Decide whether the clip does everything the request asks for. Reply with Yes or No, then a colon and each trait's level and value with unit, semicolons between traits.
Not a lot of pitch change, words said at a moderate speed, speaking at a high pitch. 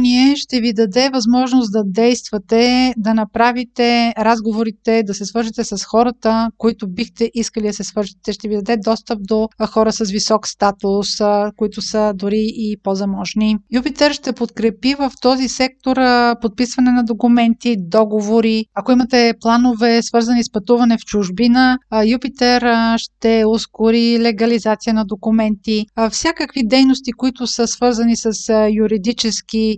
Yes: narrow, 2.0 semitones; average, 130 wpm; high, 230 Hz